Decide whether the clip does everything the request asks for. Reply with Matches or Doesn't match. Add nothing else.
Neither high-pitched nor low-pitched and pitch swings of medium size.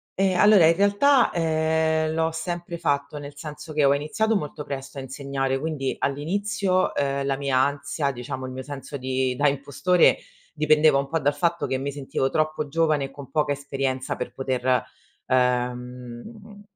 Matches